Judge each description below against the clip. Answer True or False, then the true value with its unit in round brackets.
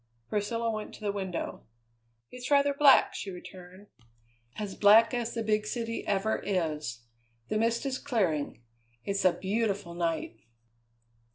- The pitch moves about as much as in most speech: True (3.9 semitones)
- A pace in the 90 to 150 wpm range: True (140 wpm)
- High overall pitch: True (205 Hz)